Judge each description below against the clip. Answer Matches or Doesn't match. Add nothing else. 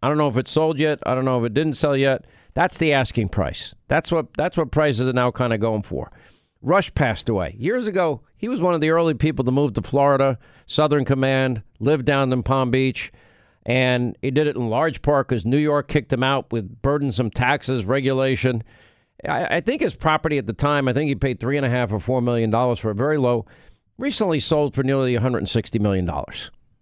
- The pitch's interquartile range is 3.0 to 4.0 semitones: Matches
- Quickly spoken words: Matches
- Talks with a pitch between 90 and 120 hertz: Doesn't match